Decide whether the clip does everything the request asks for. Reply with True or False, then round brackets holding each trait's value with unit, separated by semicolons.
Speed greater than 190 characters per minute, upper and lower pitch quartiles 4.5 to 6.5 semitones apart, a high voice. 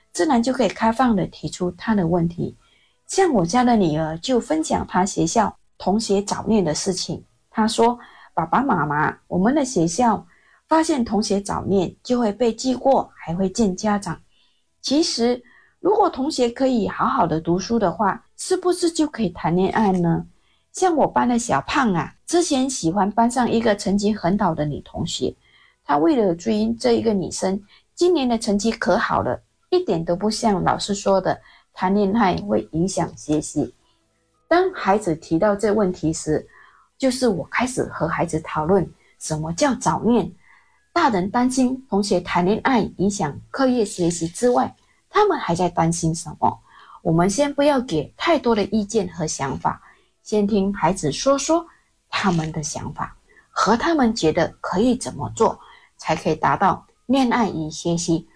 True (245 characters per minute; 6.1 semitones; 210 Hz)